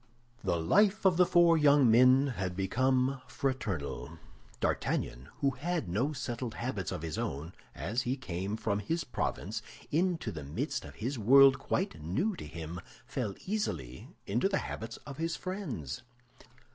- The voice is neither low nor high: No, low, 125 Hz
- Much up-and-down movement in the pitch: Yes, wide, 8.2 semitones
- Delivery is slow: No, average, 155 wpm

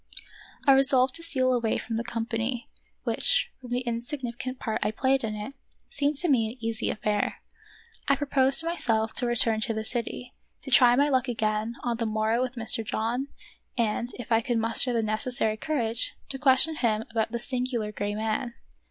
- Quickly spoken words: No, average, 190 wpm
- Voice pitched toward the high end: Yes, high, 240 Hz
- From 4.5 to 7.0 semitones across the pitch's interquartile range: No, average, 2.8 semitones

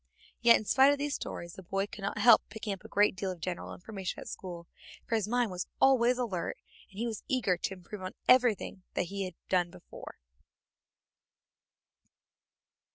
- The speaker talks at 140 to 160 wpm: No, average, 185 wpm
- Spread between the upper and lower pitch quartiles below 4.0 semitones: No, average, 4.3 semitones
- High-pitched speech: Yes, high, 200 Hz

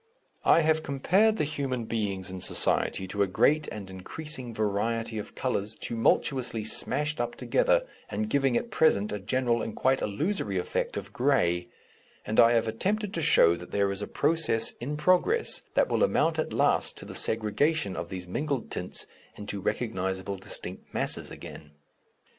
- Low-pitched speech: Yes, low, 115 Hz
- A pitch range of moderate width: No, wide, 7.3 semitones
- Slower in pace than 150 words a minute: No, average, 165 wpm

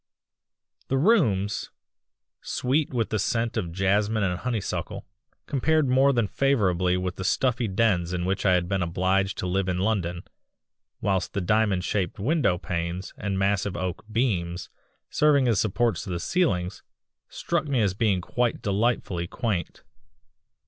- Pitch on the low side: Yes, low, 100 Hz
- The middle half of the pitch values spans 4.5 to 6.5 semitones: Yes, average, 4.8 semitones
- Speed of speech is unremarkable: Yes, average, 150 wpm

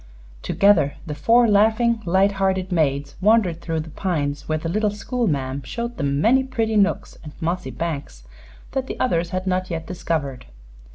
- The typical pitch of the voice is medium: Yes, medium, 180 Hz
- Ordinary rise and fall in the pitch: No, wide, 5.7 semitones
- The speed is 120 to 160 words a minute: No, average, 170 wpm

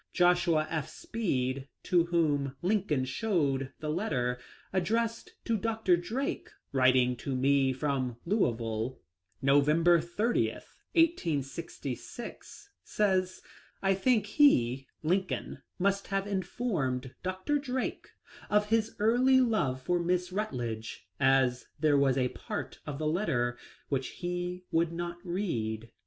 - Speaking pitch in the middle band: Yes, medium, 170 Hz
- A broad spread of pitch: Yes, wide, 7.3 semitones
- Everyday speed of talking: No, slow, 120 wpm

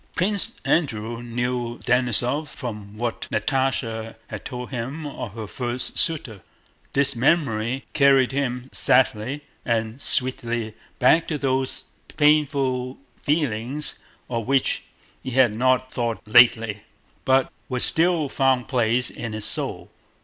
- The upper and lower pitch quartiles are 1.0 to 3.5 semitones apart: Yes, average, 2.9 semitones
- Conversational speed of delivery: No, slow, 120 wpm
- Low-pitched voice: Yes, low, 125 Hz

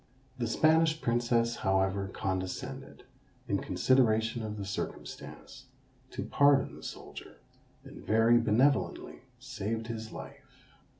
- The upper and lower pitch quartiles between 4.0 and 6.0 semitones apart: No, average, 3.4 semitones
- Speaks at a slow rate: Yes, slow, 110 wpm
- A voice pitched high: No, low, 115 Hz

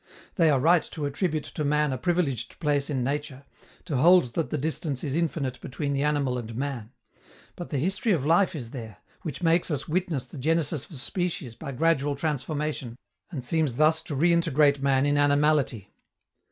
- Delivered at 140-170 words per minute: No, average, 180 wpm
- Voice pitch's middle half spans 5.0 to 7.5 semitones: No, average, 3.4 semitones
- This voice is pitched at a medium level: Yes, medium, 145 Hz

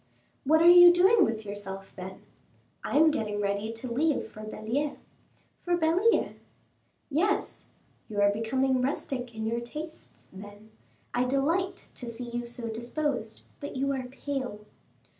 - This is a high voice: Yes, very high, 250 Hz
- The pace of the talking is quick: No, average, 145 wpm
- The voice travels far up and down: Yes, wide, 5.7 semitones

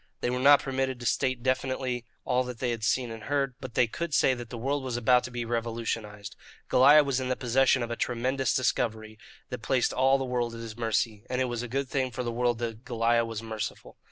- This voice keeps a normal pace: No, fast, 240 wpm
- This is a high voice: No, low, 125 Hz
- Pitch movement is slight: Yes, narrow, 2.1 semitones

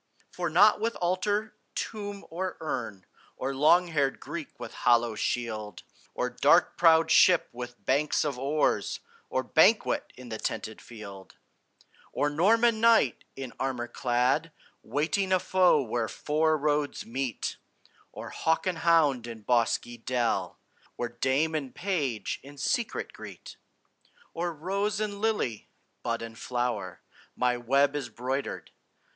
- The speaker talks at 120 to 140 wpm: Yes, slow, 135 wpm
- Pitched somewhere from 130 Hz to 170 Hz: Yes, medium, 140 Hz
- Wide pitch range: Yes, wide, 6.3 semitones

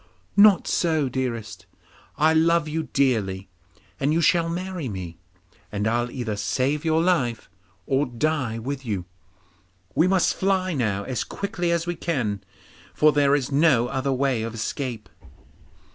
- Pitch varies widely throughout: Yes, wide, 6.0 semitones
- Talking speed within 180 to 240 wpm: No, average, 145 wpm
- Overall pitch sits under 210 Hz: Yes, medium, 140 Hz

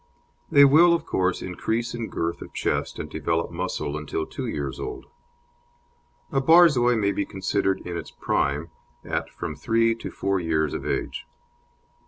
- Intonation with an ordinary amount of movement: No, wide, 6.7 semitones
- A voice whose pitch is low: Yes, low, 100 Hz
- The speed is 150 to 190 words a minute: Yes, average, 160 wpm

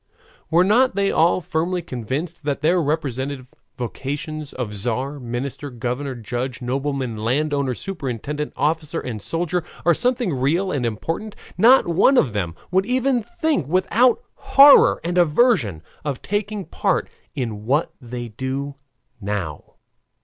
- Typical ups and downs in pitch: No, wide, 6.3 semitones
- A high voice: No, medium, 145 Hz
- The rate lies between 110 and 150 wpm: Yes, slow, 135 wpm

